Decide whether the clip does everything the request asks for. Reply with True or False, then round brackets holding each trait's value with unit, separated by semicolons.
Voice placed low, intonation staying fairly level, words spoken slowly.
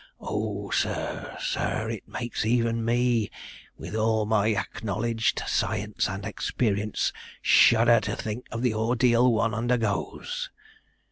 True (115 Hz; 1.9 semitones; 120 wpm)